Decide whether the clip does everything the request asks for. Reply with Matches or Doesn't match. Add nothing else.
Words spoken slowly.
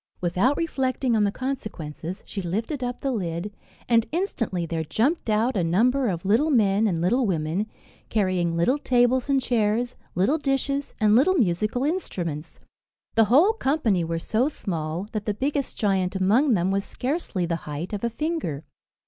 Doesn't match